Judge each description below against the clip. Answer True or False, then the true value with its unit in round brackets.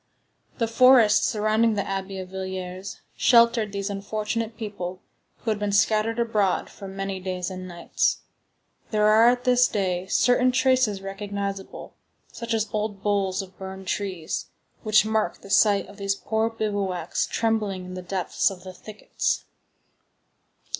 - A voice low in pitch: False (205 Hz)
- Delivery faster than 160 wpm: False (145 wpm)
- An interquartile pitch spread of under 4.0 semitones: True (2.5 semitones)